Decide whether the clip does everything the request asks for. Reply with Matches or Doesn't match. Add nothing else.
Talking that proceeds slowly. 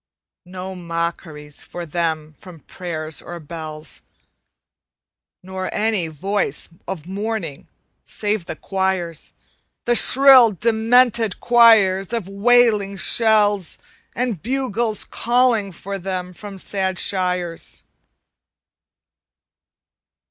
Matches